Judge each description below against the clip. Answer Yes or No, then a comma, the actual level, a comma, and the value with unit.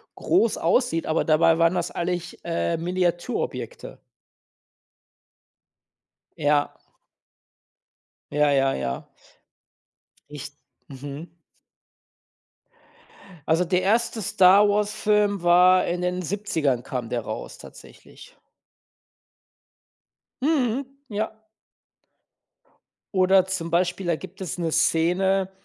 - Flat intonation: No, average, 3.5 semitones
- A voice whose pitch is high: No, medium, 180 Hz